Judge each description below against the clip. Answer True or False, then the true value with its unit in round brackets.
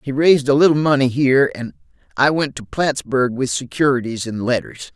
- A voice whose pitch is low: True (130 Hz)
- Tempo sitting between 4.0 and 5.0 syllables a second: False (5.4 syllables/s)